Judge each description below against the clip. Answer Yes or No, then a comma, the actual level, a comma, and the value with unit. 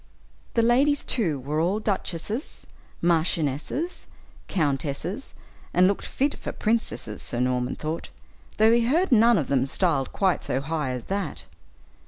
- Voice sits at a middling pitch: Yes, medium, 175 Hz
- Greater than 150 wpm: No, average, 140 wpm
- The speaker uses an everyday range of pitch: No, wide, 8.4 semitones